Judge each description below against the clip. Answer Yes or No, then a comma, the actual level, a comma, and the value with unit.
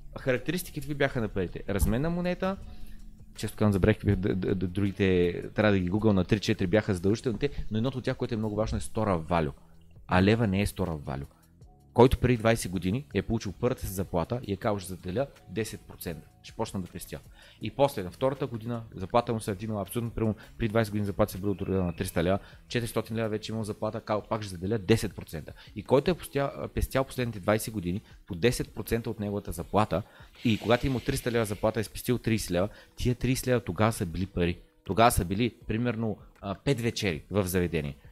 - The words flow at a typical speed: No, fast, 215 wpm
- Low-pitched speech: Yes, low, 105 Hz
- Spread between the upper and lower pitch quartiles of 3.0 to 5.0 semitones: Yes, average, 3.5 semitones